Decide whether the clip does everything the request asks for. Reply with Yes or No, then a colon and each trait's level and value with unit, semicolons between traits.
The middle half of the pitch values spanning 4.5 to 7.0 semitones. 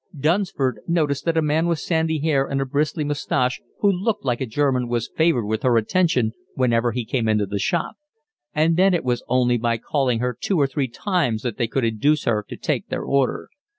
Yes: average, 5.1 semitones